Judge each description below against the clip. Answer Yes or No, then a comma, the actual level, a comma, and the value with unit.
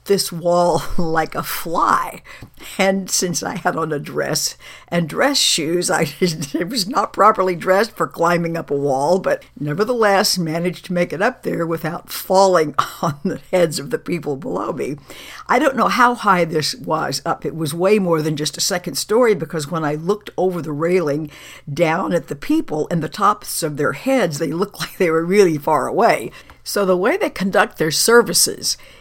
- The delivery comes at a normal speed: Yes, average, 190 wpm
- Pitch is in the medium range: Yes, medium, 175 Hz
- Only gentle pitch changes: No, average, 3.4 semitones